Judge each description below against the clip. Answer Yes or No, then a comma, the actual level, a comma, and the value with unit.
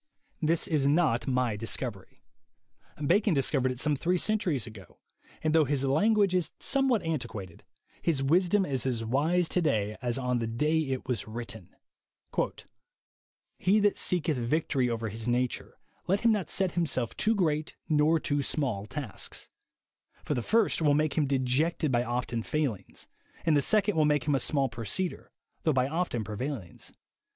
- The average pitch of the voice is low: No, medium, 145 Hz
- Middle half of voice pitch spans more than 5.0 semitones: Yes, wide, 5.5 semitones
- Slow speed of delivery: No, average, 165 wpm